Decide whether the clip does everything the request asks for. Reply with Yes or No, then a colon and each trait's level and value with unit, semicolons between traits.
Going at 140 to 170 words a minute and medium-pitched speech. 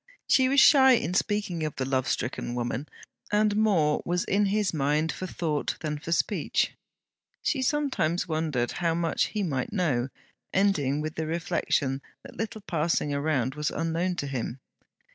Yes: average, 165 wpm; medium, 160 Hz